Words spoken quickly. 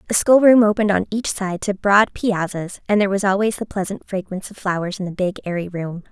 Yes: fast, 225 wpm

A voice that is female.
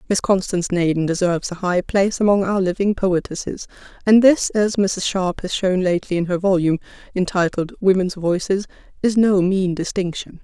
Yes: female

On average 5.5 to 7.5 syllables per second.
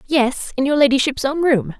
No: 5.0 syllables/s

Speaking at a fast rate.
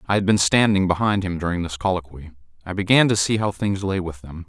Yes: fast, 240 wpm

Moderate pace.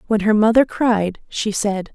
Yes: average, 185 wpm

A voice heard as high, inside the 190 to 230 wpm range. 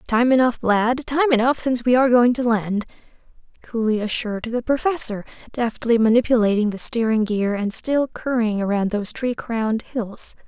No: high, 230 Hz; average, 160 wpm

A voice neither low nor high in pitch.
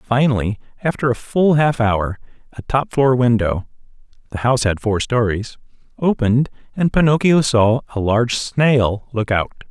No: low, 120 Hz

